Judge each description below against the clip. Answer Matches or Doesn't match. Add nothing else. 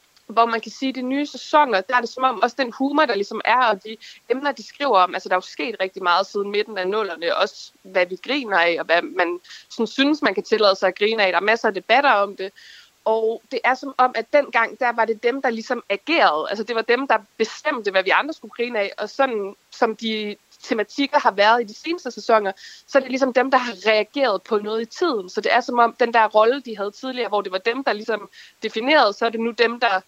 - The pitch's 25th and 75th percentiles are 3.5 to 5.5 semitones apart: Matches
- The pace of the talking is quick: Matches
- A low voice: Doesn't match